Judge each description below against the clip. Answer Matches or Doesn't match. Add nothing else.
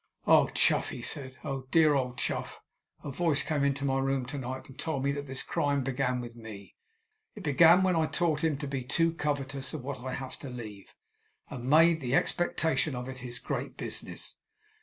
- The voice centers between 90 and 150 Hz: Matches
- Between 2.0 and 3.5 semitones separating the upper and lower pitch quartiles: Matches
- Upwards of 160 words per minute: Matches